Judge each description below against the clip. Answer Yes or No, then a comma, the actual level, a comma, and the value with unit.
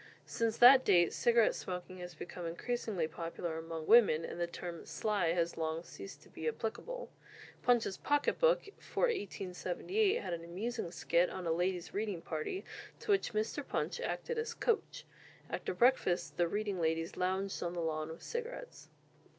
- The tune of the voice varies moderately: No, wide, 6.3 semitones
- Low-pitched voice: No, medium, 185 Hz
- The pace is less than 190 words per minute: Yes, average, 165 wpm